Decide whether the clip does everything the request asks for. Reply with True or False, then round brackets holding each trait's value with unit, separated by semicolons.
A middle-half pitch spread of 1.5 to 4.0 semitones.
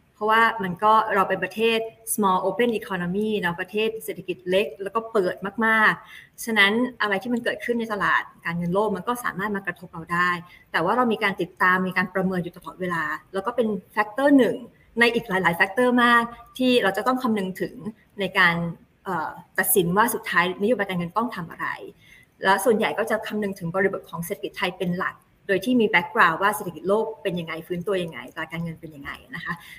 True (3.4 semitones)